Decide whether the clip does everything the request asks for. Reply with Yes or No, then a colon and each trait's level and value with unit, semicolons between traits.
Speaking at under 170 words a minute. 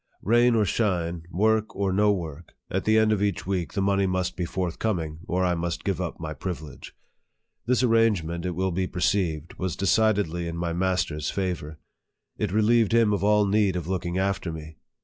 No: average, 190 wpm